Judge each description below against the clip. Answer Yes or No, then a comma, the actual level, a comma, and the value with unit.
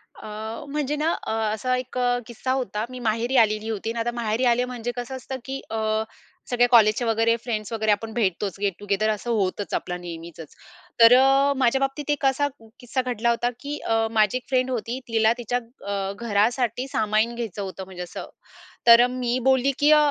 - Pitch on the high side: Yes, high, 230 Hz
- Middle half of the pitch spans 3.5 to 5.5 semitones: No, average, 2.9 semitones